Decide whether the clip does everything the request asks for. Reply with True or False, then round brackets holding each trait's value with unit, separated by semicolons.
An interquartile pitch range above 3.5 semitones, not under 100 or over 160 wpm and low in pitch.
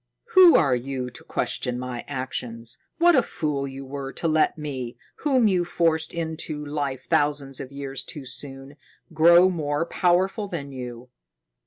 False (4.2 semitones; 155 wpm; 145 Hz)